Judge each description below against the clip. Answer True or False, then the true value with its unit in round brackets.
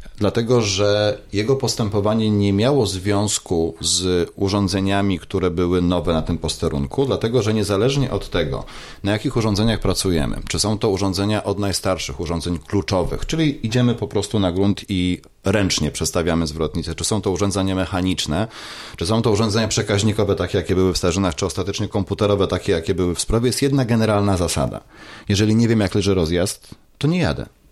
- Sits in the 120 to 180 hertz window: False (100 Hz)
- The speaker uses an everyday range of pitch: True (3.1 semitones)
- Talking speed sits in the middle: False (170 wpm)